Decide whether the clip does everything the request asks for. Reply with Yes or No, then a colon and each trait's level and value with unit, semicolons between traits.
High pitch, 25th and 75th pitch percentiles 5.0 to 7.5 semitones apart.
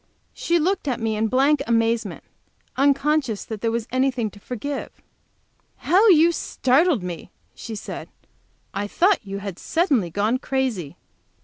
Yes: very high, 250 Hz; wide, 5.6 semitones